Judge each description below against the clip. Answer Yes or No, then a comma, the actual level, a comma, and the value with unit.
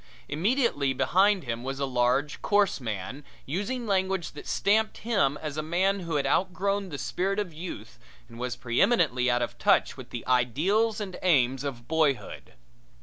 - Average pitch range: No, wide, 7.0 semitones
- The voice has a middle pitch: Yes, medium, 155 Hz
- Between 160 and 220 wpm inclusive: Yes, average, 165 wpm